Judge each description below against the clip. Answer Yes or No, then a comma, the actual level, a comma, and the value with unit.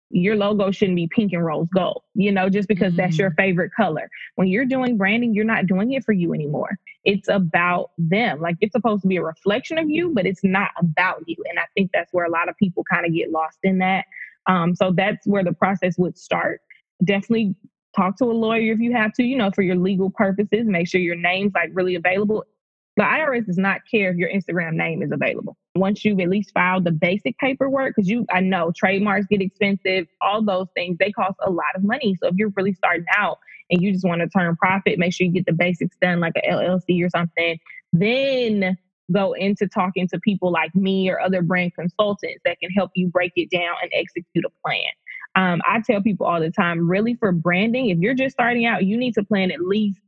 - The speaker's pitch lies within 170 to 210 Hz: Yes, high, 190 Hz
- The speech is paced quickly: Yes, fast, 230 wpm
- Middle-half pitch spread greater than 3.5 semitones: No, average, 2.8 semitones